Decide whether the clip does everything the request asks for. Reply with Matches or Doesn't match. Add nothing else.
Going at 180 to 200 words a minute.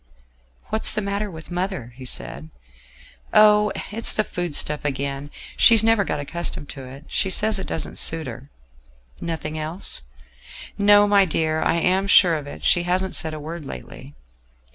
Doesn't match